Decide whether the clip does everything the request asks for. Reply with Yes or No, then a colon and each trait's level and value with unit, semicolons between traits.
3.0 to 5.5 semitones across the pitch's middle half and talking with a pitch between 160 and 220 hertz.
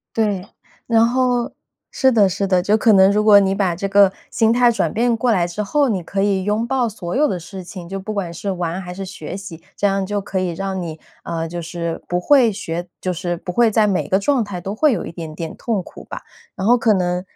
Yes: average, 3.7 semitones; high, 195 Hz